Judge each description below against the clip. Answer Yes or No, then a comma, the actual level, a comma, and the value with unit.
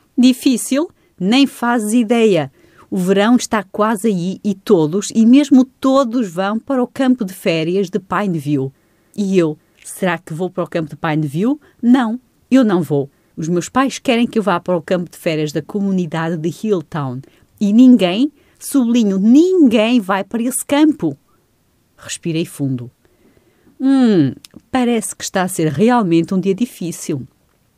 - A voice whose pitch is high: Yes, high, 200 Hz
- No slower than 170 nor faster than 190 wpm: No, average, 155 wpm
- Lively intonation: Yes, wide, 6.4 semitones